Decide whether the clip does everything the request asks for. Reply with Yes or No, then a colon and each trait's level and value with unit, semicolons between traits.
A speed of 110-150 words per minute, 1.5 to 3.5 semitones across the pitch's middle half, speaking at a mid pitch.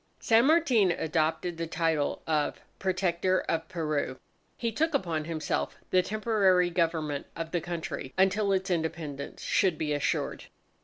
Yes: average, 145 wpm; average, 3.2 semitones; medium, 170 Hz